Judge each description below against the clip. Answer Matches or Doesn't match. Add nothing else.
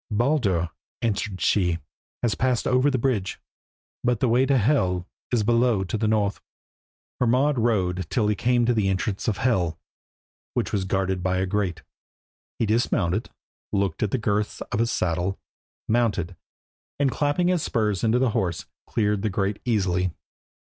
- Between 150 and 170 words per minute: Matches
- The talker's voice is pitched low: Matches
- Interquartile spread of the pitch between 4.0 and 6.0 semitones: Matches